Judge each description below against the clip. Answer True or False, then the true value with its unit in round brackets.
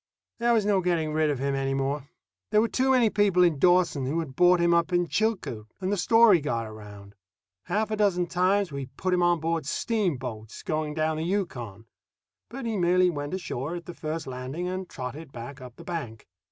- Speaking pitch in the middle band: True (170 Hz)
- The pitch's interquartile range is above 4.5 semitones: True (5.4 semitones)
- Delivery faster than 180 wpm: True (205 wpm)